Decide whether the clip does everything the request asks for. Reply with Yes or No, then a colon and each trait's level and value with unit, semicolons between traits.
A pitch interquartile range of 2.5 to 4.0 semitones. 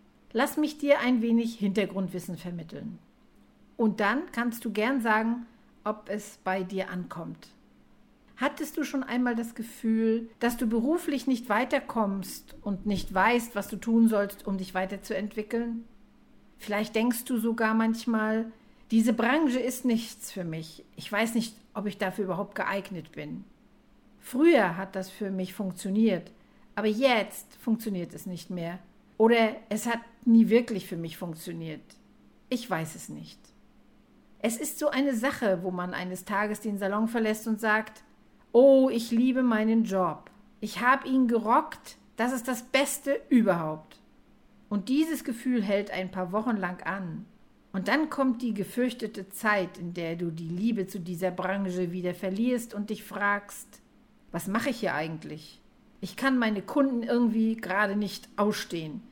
Yes: average, 3.7 semitones